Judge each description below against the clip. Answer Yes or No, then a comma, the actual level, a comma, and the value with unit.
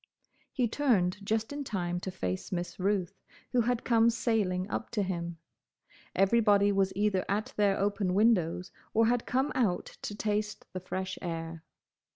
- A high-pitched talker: Yes, high, 200 Hz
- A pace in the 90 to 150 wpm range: No, average, 160 wpm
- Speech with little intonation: No, average, 3.8 semitones